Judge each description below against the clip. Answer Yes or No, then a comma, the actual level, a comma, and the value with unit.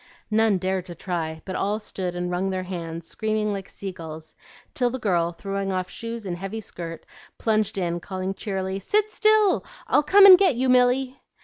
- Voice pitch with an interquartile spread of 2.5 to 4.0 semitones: No, average, 4.4 semitones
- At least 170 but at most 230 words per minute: Yes, average, 190 wpm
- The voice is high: Yes, high, 195 Hz